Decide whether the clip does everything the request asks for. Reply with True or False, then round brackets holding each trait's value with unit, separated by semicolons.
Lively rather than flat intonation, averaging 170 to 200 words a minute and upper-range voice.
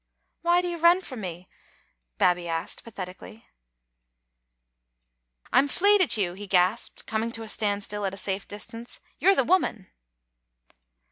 False (5.7 semitones; 150 wpm; 205 Hz)